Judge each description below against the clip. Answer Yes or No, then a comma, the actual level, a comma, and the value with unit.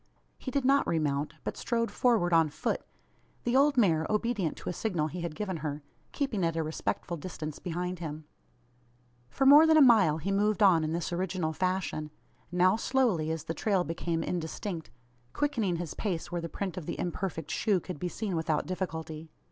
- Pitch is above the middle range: No, medium, 180 Hz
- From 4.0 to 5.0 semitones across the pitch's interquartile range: Yes, average, 4.7 semitones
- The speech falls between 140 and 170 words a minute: No, average, 190 wpm